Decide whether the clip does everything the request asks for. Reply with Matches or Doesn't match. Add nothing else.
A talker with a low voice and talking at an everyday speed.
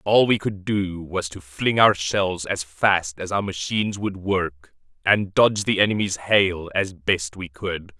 Matches